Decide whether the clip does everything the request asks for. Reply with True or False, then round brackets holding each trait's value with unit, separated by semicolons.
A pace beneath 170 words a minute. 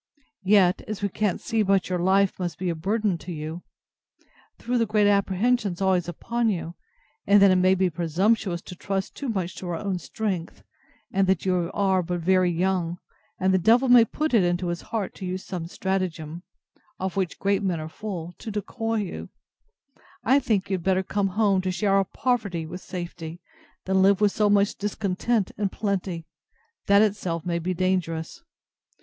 False (190 wpm)